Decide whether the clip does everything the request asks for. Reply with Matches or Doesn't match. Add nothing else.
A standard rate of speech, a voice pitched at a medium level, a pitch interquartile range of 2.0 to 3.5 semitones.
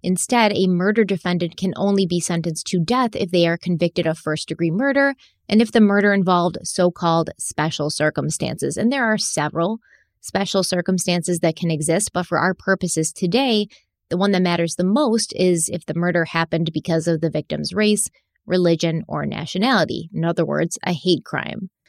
Matches